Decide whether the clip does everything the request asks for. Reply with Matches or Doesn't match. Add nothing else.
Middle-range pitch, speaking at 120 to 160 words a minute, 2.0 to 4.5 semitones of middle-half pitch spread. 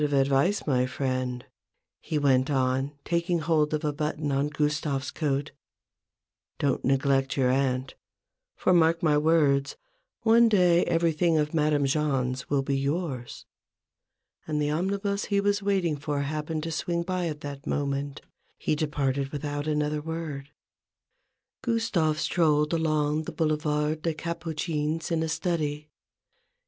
Matches